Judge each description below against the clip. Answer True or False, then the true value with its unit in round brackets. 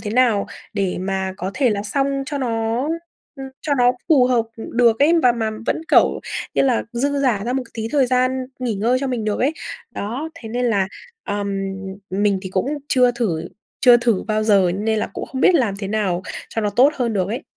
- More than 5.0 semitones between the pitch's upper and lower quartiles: False (3.8 semitones)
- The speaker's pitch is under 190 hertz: False (235 Hz)